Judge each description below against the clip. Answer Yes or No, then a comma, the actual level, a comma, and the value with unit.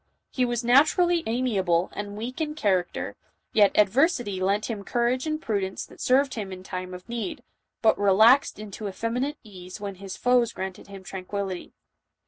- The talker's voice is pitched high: Yes, high, 215 Hz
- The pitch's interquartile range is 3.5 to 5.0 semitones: Yes, average, 4.6 semitones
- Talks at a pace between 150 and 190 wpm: Yes, average, 160 wpm